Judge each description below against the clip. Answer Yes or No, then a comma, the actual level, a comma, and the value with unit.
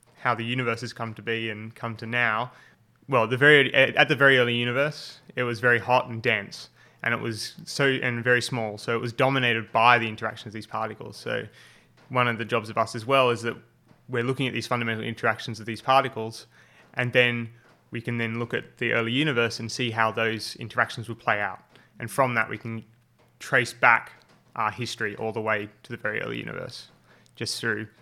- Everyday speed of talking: No, fast, 210 wpm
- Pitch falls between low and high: No, low, 115 Hz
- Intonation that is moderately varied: No, narrow, 1.8 semitones